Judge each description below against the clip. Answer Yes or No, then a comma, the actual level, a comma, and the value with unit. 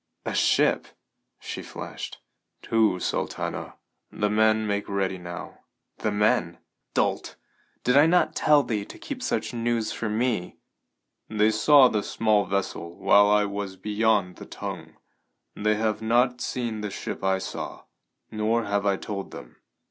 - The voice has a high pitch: No, low, 105 Hz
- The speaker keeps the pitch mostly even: Yes, narrow, 2.1 semitones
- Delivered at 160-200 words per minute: No, average, 150 wpm